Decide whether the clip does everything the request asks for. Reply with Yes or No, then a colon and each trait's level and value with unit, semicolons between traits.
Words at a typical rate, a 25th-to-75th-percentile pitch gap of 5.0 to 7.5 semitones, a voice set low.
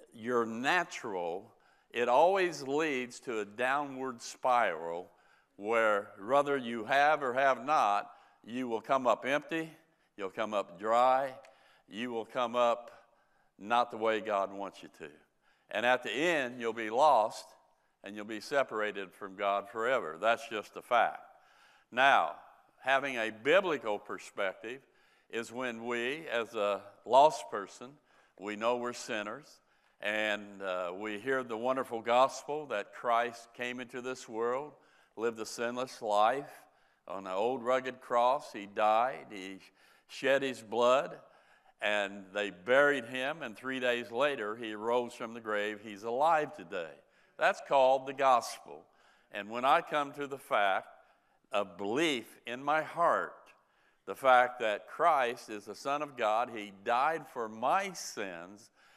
No: average, 145 wpm; average, 3.8 semitones; low, 120 Hz